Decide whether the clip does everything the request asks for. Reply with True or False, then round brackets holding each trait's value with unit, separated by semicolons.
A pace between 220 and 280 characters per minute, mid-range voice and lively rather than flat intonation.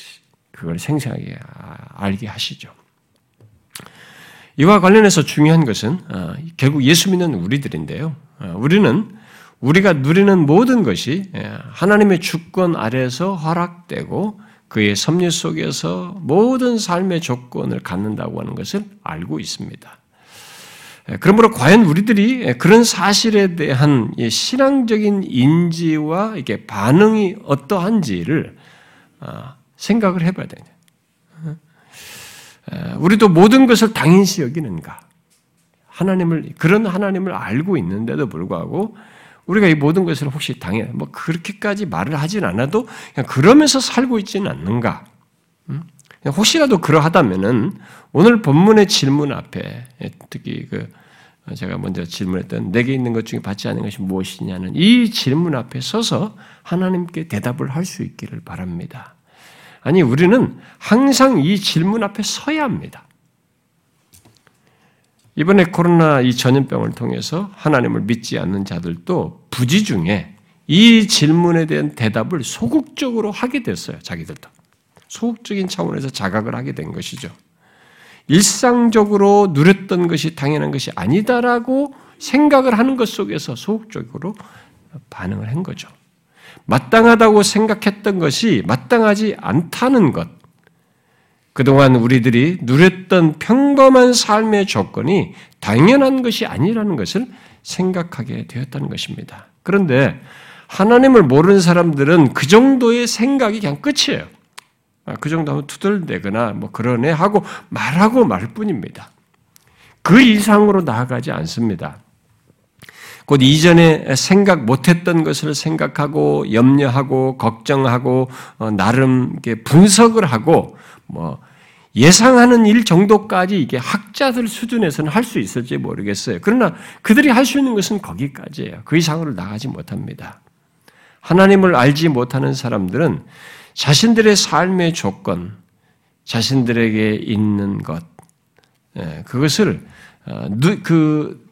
True (275 characters per minute; 175 Hz; 7.2 semitones)